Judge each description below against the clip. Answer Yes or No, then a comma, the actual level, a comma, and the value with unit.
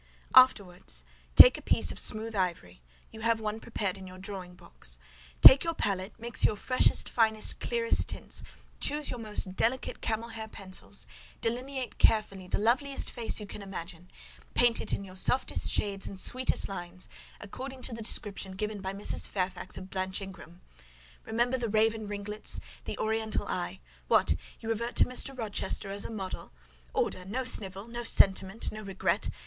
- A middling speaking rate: Yes, average, 160 wpm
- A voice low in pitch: No, high, 210 Hz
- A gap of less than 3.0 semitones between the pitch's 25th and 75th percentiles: No, average, 3.5 semitones